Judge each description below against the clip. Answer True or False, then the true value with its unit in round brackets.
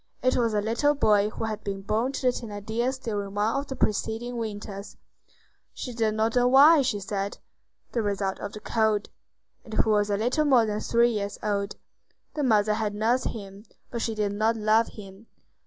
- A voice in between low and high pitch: False (220 Hz)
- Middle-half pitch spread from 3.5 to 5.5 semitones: False (2.6 semitones)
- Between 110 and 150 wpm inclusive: False (190 wpm)